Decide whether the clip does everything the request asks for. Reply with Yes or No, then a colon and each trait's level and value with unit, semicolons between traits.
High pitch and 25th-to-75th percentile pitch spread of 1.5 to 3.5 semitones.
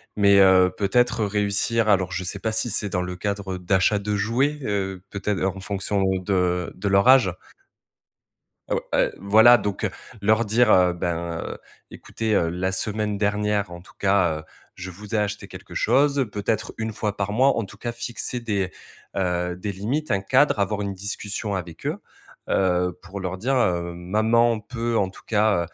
No: low, 100 Hz; average, 2.8 semitones